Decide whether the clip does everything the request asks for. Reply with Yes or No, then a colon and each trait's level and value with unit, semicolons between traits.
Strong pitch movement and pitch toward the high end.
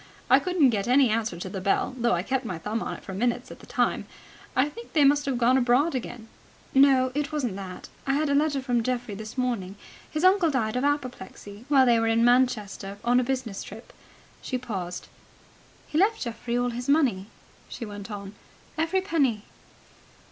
No: average, 4.4 semitones; high, 245 Hz